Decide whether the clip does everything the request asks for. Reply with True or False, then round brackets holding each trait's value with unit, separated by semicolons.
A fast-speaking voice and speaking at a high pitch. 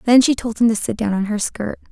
True (315 wpm; 220 Hz)